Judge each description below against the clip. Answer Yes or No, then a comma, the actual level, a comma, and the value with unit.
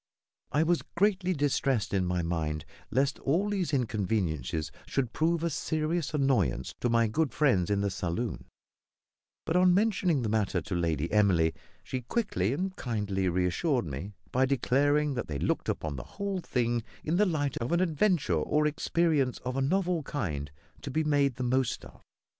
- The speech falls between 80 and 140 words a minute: No, average, 170 wpm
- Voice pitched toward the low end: Yes, low, 130 Hz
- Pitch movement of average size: No, wide, 8.6 semitones